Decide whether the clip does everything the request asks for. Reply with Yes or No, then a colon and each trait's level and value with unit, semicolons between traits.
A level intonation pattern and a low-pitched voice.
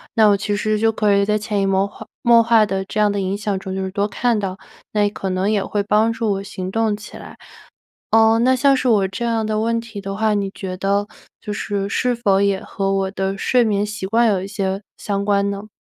No: narrow, 2.0 semitones; high, 205 Hz